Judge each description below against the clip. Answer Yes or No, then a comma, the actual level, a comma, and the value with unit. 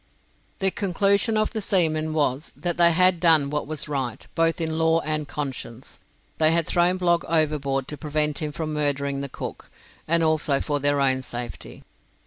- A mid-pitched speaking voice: Yes, medium, 155 Hz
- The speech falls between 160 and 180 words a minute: Yes, average, 175 wpm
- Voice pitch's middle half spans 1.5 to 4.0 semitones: Yes, average, 2.9 semitones